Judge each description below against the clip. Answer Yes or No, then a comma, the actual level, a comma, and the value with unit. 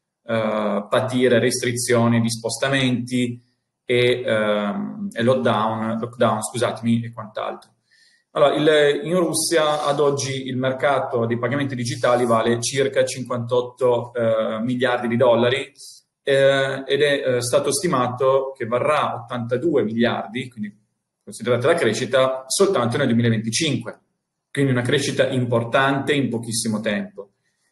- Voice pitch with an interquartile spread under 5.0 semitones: Yes, average, 2.7 semitones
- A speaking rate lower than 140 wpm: Yes, average, 120 wpm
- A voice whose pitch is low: Yes, low, 125 Hz